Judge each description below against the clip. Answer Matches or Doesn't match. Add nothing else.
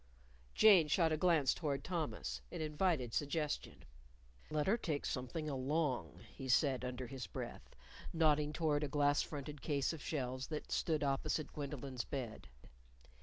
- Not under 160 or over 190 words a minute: Doesn't match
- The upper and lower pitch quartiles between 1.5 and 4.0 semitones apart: Matches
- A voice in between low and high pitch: Matches